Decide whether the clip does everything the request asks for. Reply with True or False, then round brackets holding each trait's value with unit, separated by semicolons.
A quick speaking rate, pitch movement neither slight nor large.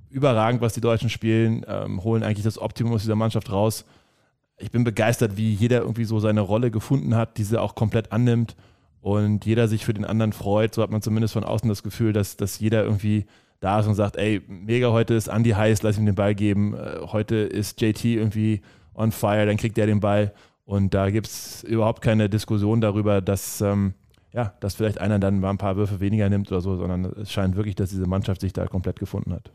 False (220 wpm; 1.7 semitones)